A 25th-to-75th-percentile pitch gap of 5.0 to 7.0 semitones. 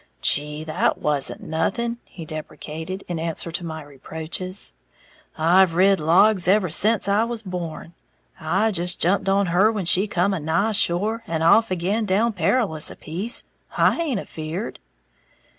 No: average, 4.1 semitones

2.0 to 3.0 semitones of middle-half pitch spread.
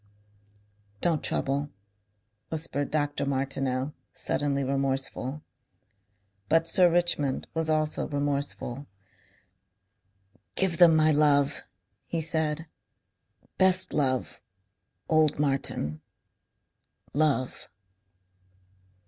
Yes: narrow, 2.6 semitones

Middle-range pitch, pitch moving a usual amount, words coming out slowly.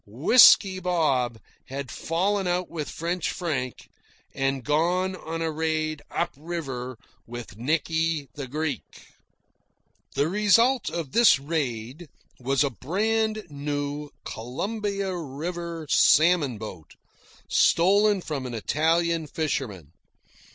Yes: medium, 155 Hz; average, 4.7 semitones; slow, 110 wpm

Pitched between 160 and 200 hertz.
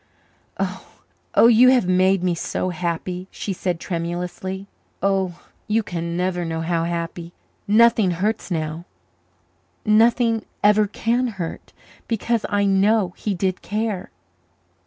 Yes: high, 190 Hz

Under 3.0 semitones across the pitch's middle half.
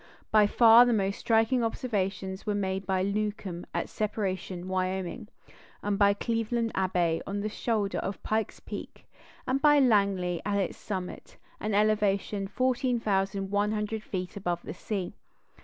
Yes: narrow, 2.5 semitones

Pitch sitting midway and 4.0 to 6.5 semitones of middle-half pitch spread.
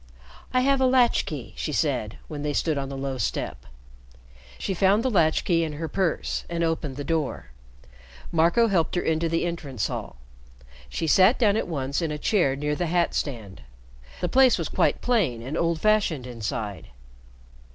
Yes: medium, 160 Hz; average, 5.2 semitones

